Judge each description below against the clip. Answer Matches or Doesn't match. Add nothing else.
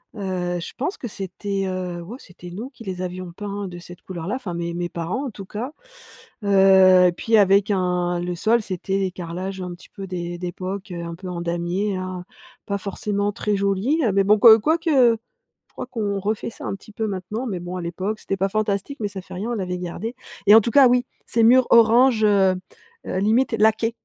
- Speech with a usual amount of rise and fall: Matches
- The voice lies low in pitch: Doesn't match